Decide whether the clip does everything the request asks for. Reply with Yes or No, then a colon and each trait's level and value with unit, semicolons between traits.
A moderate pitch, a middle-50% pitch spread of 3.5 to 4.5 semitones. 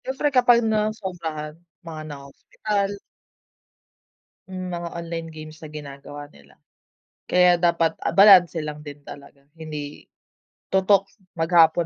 Yes: medium, 165 Hz; average, 4.1 semitones